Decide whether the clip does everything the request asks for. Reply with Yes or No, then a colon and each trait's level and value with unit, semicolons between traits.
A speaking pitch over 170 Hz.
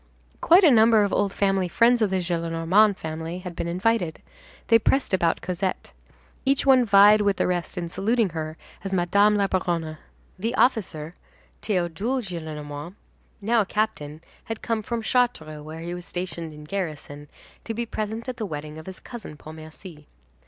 Yes: medium, 185 Hz